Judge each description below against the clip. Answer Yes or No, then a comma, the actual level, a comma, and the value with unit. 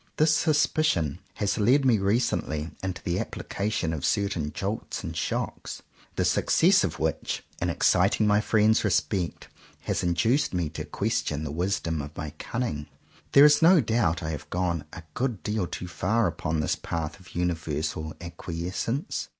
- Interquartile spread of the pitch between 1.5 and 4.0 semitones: No, wide, 5.6 semitones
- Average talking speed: Yes, average, 160 wpm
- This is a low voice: Yes, very low, 90 Hz